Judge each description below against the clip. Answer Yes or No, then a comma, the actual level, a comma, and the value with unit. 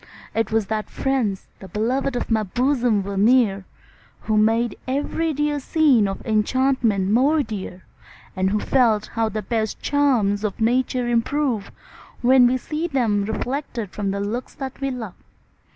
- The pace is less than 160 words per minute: Yes, average, 150 wpm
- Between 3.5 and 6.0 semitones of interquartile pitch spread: Yes, average, 4.0 semitones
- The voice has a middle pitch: No, high, 230 Hz